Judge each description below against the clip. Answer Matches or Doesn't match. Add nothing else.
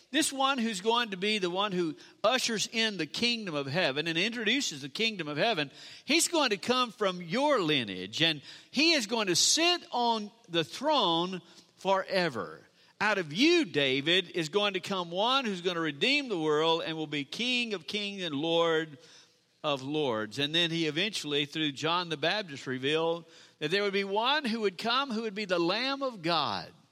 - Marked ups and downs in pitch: Matches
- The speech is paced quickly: Doesn't match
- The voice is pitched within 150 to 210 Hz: Matches